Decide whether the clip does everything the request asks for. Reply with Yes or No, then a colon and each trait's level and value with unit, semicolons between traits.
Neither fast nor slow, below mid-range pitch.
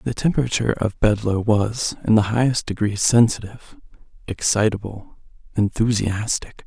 No: slow, 110 wpm; low, 110 Hz